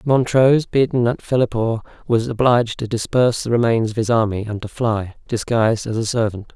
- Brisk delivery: No, average, 185 wpm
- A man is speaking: Yes, male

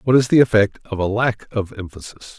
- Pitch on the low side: Yes, low, 110 Hz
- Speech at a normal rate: No, fast, 225 wpm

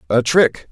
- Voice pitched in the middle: No, low, 130 Hz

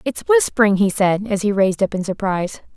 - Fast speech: Yes, fast, 215 wpm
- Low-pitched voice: No, high, 195 Hz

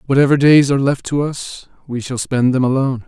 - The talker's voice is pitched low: Yes, low, 130 Hz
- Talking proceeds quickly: Yes, fast, 215 wpm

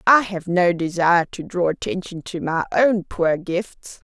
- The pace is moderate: Yes, average, 175 wpm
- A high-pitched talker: No, medium, 180 Hz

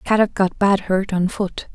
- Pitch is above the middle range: Yes, high, 195 Hz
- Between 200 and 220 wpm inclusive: Yes, fast, 205 wpm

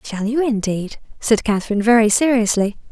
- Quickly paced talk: No, average, 145 wpm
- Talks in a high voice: Yes, high, 225 Hz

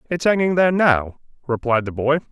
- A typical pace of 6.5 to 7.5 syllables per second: No, 5.8 syllables/s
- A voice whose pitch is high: No, medium, 145 Hz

